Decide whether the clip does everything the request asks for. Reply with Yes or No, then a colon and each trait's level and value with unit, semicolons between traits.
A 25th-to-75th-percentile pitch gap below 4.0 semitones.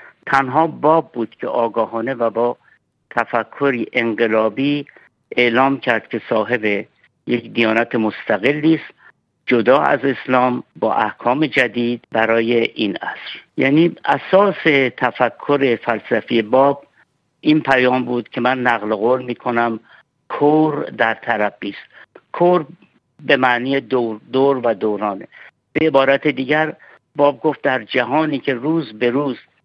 Yes: average, 3.5 semitones